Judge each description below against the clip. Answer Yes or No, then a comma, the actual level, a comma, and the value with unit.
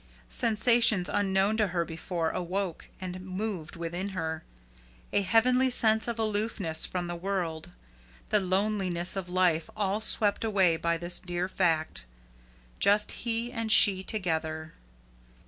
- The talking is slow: Yes, slow, 130 wpm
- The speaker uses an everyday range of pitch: Yes, average, 3.7 semitones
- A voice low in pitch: No, high, 190 Hz